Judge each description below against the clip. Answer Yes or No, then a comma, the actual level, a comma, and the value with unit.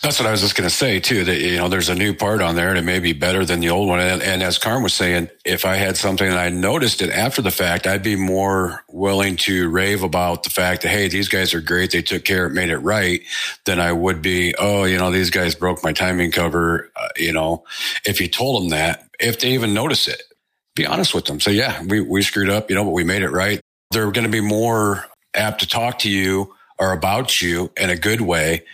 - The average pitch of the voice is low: Yes, very low, 95 Hz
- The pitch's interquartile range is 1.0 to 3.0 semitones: Yes, narrow, 2.4 semitones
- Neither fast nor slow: No, fast, 265 wpm